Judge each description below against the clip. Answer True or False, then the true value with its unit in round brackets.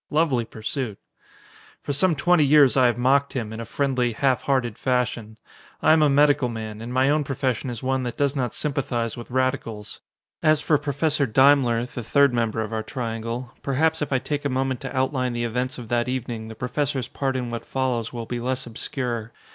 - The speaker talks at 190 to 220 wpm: True (205 wpm)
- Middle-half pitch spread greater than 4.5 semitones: False (2.9 semitones)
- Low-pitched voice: True (130 Hz)